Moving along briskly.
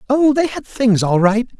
Yes: fast, 225 wpm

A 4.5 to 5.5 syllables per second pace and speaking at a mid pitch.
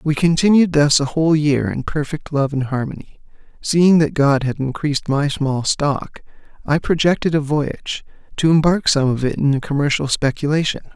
Yes: 5.1 syllables/s; medium, 145 Hz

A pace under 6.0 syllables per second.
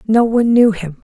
Yes: 5.5 syllables/s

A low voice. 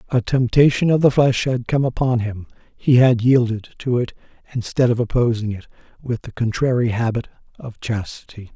Yes: low, 120 Hz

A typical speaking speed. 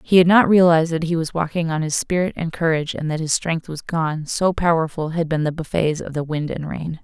No: fast, 255 wpm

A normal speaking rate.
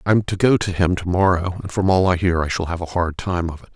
No: fast, 335 wpm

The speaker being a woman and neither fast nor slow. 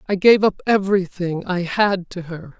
Yes: female; average, 185 wpm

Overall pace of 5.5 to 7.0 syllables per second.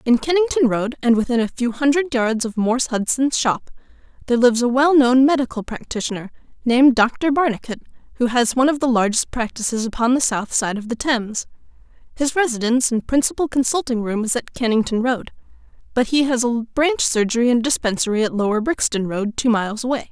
Yes: 5.9 syllables/s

